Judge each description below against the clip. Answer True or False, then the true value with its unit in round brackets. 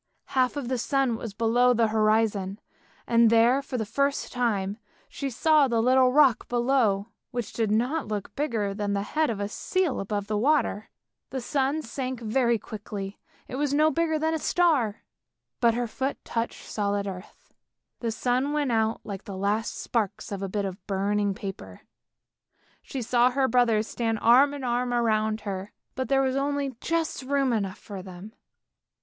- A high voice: True (235 Hz)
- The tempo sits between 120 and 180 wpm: True (175 wpm)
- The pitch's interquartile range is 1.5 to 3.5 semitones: False (4.4 semitones)